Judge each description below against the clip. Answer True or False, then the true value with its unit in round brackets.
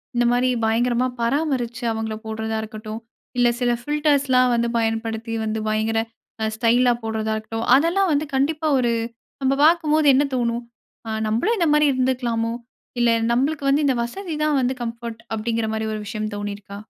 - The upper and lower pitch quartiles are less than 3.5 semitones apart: False (3.8 semitones)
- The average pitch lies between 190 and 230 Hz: False (240 Hz)